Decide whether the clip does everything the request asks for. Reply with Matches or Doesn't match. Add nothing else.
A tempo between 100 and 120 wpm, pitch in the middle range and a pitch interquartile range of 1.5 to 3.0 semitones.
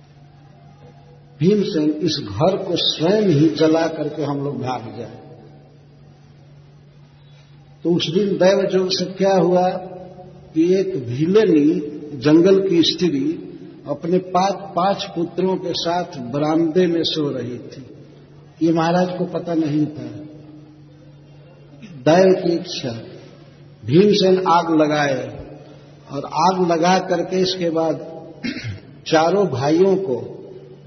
Doesn't match